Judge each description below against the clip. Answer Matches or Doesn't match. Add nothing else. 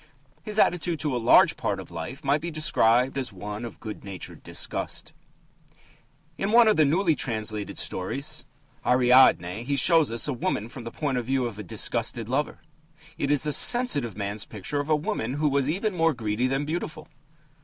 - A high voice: Doesn't match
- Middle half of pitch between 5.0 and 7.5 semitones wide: Matches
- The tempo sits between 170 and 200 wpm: Matches